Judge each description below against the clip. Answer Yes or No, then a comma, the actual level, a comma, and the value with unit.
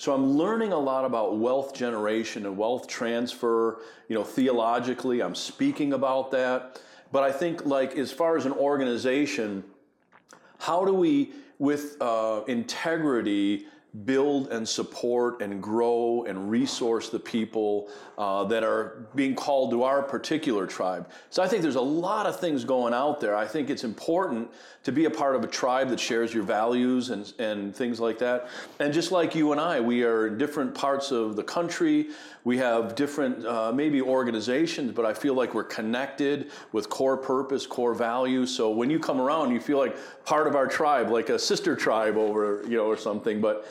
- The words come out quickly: No, average, 185 wpm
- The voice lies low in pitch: Yes, low, 125 Hz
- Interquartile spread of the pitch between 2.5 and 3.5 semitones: No, average, 4.1 semitones